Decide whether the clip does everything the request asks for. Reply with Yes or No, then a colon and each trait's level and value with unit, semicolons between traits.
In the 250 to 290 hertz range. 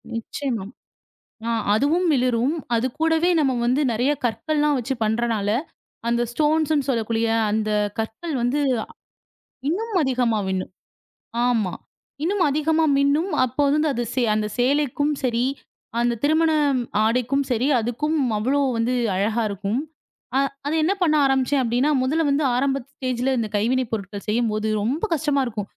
Yes: very high, 255 Hz